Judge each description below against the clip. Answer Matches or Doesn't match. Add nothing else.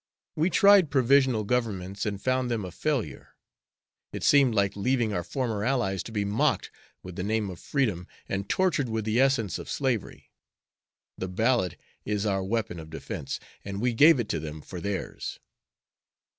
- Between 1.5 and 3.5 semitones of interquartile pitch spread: Doesn't match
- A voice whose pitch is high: Doesn't match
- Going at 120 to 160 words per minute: Doesn't match